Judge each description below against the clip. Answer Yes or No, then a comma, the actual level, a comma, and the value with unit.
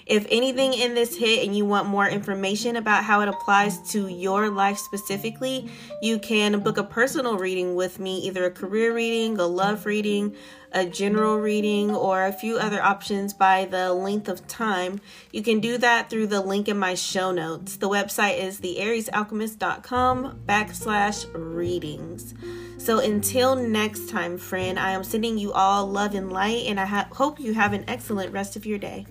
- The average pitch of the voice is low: No, high, 205 Hz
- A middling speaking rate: Yes, average, 180 wpm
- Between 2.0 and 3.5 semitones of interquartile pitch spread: Yes, narrow, 2.6 semitones